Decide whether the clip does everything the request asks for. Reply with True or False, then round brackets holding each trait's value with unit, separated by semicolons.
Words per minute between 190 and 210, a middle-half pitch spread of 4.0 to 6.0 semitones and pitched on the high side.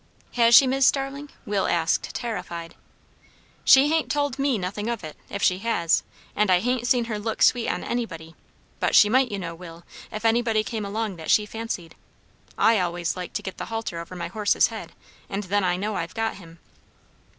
True (195 wpm; 4.9 semitones; 210 Hz)